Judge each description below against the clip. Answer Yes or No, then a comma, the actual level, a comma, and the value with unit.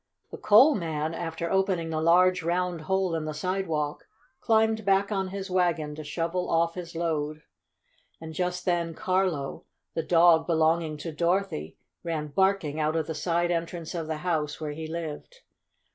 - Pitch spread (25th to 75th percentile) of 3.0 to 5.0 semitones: No, narrow, 2.6 semitones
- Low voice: No, medium, 170 Hz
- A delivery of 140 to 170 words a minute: Yes, average, 165 wpm